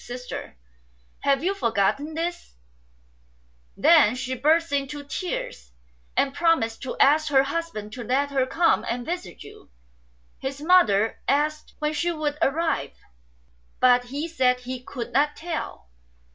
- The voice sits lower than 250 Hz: No, very high, 275 Hz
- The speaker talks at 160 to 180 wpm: No, average, 140 wpm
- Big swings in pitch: No, average, 4.3 semitones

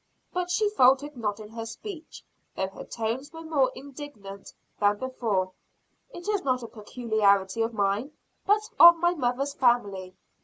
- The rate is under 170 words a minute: Yes, average, 155 wpm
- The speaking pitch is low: No, high, 245 Hz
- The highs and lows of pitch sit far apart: Yes, wide, 6.2 semitones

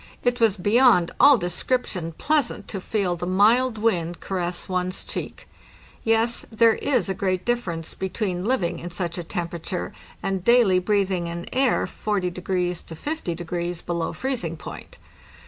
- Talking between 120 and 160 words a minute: Yes, average, 145 wpm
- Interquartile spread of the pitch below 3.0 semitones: No, average, 4.6 semitones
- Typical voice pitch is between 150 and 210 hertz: Yes, medium, 185 Hz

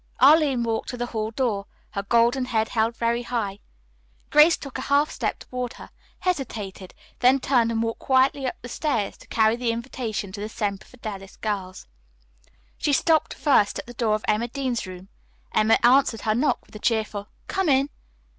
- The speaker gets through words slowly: No, average, 185 wpm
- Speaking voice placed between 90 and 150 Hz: No, high, 235 Hz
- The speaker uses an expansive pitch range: No, average, 3.6 semitones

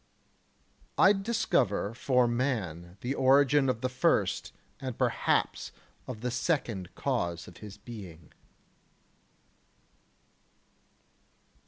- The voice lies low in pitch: Yes, low, 120 Hz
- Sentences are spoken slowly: Yes, slow, 100 wpm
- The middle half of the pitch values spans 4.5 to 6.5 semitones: Yes, wide, 5.4 semitones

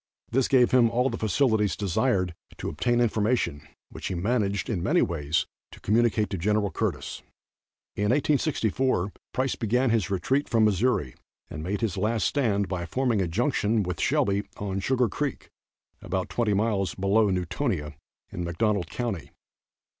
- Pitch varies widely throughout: No, average, 4.4 semitones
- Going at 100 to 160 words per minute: Yes, average, 155 wpm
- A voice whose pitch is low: Yes, low, 105 Hz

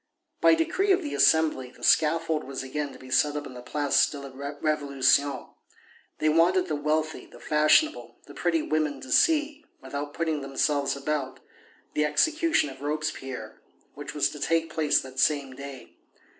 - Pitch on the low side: No, medium, 150 Hz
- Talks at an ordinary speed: Yes, average, 170 wpm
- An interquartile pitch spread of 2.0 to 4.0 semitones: Yes, narrow, 2.5 semitones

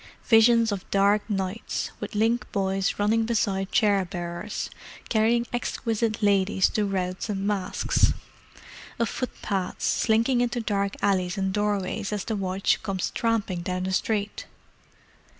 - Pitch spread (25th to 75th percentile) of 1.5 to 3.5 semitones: Yes, narrow, 2.6 semitones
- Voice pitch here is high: Yes, high, 205 Hz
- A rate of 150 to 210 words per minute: No, slow, 135 wpm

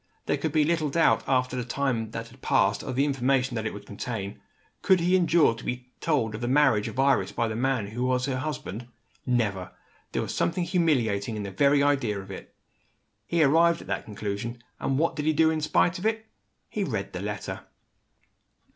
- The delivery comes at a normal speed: No, fast, 210 wpm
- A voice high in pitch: No, low, 130 Hz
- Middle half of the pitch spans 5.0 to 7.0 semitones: Yes, wide, 5.5 semitones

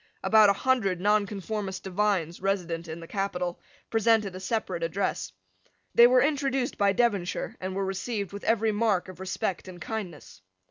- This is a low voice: No, high, 200 Hz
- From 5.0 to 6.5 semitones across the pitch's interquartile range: No, average, 3.2 semitones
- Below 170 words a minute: Yes, average, 155 wpm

